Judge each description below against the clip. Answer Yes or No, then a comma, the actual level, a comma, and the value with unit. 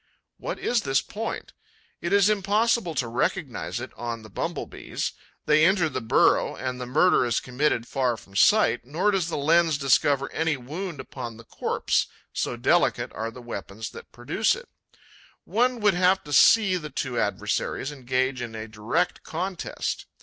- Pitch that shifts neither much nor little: No, wide, 7.2 semitones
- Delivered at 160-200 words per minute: Yes, average, 170 wpm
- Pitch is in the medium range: Yes, medium, 145 Hz